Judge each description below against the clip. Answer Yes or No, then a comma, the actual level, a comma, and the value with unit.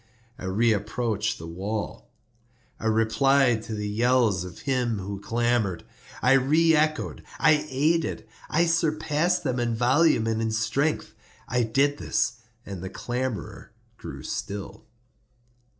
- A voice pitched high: No, low, 120 Hz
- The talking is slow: Yes, slow, 120 wpm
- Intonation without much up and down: No, average, 4.7 semitones